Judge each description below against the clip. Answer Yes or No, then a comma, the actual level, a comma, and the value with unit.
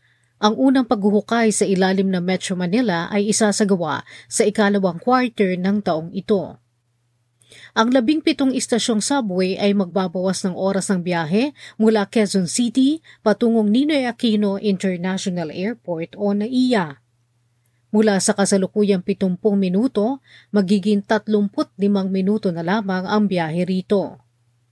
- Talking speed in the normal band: Yes, average, 125 wpm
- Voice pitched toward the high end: Yes, high, 200 Hz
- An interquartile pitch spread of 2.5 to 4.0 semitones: Yes, average, 3.0 semitones